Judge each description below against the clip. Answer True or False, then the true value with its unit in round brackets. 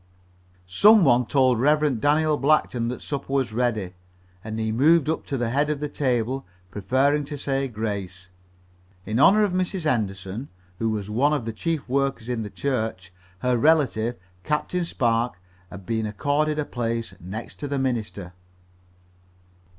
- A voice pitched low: True (125 Hz)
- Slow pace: False (160 wpm)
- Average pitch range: True (4.8 semitones)